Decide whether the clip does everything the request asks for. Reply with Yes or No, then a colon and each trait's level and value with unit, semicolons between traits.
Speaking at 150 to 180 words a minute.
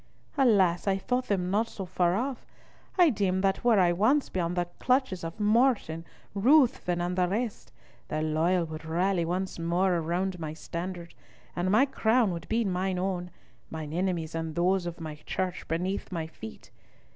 Yes: average, 170 wpm